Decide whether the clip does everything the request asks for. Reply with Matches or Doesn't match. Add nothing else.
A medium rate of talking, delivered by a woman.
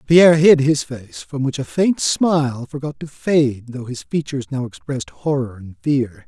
Doesn't match